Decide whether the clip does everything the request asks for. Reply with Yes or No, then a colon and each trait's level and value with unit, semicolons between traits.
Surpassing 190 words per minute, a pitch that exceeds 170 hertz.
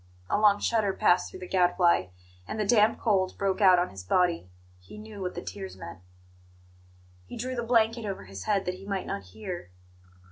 Yes: average, 200 wpm; high, 190 Hz